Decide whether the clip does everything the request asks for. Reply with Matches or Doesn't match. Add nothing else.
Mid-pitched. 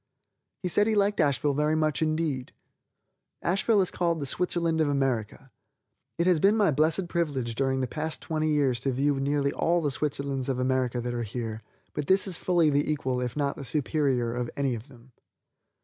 Matches